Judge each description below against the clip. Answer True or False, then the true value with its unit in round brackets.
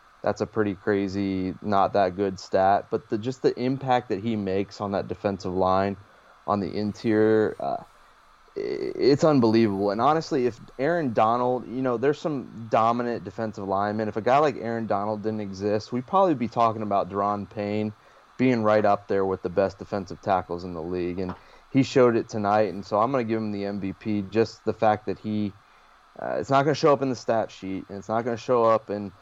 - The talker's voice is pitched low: True (105 Hz)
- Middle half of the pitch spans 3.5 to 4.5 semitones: False (2.8 semitones)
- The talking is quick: True (210 wpm)